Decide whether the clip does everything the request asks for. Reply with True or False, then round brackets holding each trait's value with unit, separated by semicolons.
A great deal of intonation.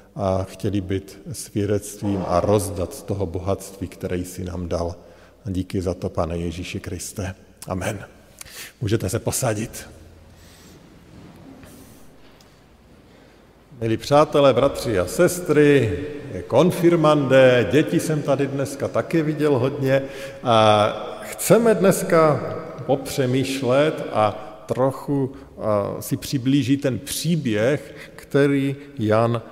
True (6.5 semitones)